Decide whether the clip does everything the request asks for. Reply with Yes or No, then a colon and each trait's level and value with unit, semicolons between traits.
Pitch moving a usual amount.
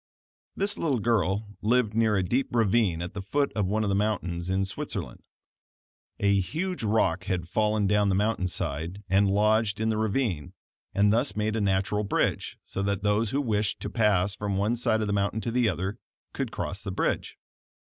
No: narrow, 2.3 semitones